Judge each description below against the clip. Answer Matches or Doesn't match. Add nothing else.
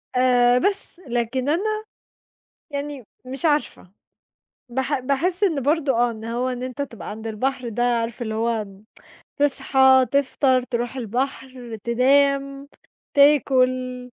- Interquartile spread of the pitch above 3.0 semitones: Doesn't match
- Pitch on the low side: Doesn't match